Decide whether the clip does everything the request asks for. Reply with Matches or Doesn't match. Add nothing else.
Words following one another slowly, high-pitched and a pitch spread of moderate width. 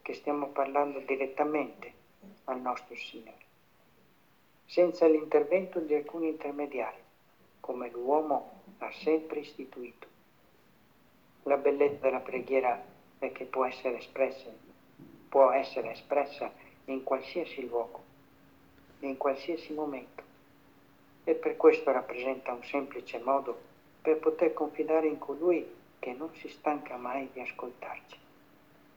Doesn't match